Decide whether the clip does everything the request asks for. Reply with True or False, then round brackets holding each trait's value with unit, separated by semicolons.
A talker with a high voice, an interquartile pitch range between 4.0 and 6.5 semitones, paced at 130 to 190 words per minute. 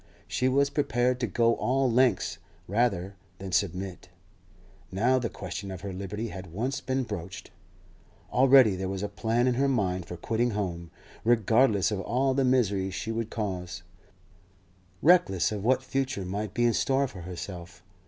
False (110 Hz; 5.1 semitones; 165 wpm)